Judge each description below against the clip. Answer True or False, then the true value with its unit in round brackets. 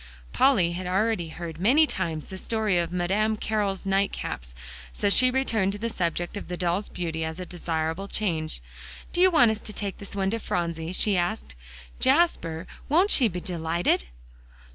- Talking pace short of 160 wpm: False (175 wpm)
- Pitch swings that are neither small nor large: True (4.2 semitones)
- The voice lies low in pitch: False (190 Hz)